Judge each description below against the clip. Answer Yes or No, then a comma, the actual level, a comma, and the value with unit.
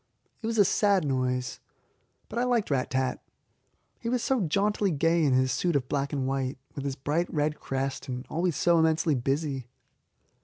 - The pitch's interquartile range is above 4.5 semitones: Yes, average, 5.2 semitones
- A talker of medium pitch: Yes, medium, 150 Hz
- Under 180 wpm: No, average, 185 wpm